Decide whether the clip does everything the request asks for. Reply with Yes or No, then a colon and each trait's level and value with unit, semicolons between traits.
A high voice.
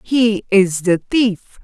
Yes: high, 205 Hz